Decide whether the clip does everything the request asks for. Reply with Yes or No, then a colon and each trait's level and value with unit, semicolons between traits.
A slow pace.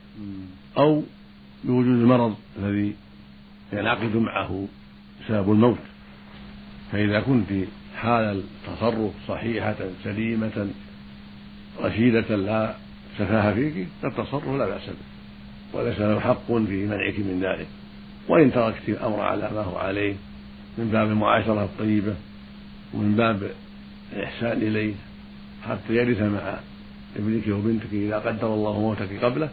No: average, 110 wpm